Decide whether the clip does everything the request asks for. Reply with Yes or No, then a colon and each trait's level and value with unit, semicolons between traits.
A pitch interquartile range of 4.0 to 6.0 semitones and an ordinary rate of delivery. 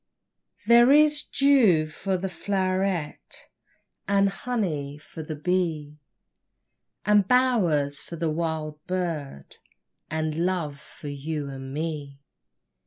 No: average, 4.6 semitones; slow, 105 wpm